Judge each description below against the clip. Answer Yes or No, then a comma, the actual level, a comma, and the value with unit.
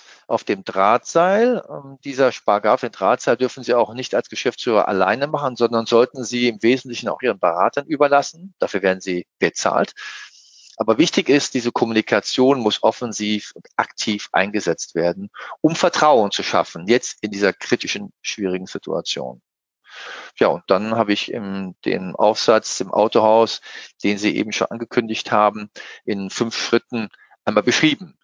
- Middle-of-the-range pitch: No, low, 115 Hz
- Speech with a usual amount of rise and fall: Yes, average, 3.9 semitones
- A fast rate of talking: No, average, 150 wpm